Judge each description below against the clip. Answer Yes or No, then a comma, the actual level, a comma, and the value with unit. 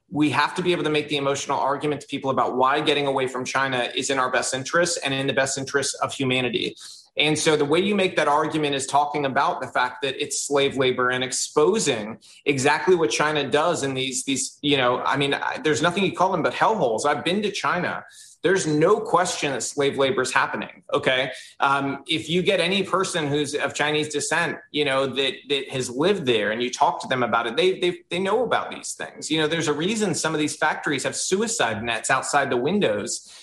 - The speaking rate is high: Yes, fast, 230 wpm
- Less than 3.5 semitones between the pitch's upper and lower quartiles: Yes, narrow, 2.5 semitones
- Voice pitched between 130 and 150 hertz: Yes, medium, 140 Hz